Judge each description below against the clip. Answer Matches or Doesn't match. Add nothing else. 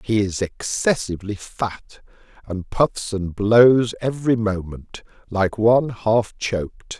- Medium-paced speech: Doesn't match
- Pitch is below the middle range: Matches